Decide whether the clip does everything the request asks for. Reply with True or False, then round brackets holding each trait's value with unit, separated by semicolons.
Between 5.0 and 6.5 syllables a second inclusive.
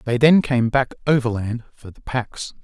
False (4.5 syllables/s)